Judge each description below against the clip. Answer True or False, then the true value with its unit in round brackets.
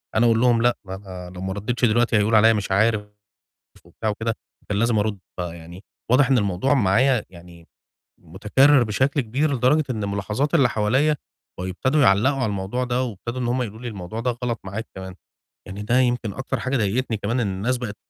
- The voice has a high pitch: False (115 Hz)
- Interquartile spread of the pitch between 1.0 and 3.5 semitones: False (4.0 semitones)